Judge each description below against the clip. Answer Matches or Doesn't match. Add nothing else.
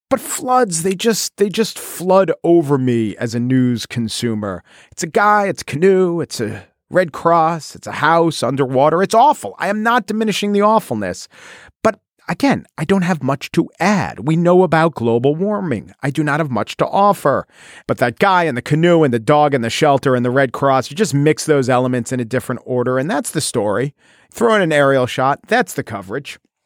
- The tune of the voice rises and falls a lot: Matches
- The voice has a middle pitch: Matches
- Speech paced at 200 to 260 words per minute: Matches